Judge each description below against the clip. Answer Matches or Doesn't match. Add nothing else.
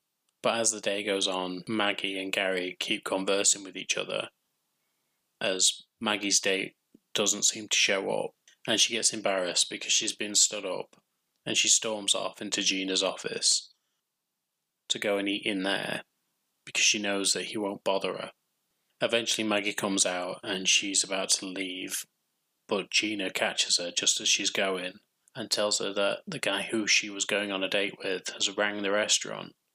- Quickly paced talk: Doesn't match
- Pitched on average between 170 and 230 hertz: Doesn't match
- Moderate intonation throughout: Doesn't match